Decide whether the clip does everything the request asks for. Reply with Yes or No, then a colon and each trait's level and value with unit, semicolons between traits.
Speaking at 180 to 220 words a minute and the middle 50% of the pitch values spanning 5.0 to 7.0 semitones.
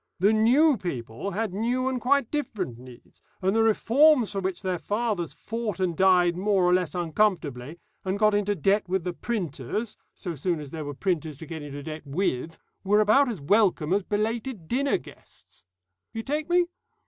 Yes: average, 185 wpm; wide, 5.4 semitones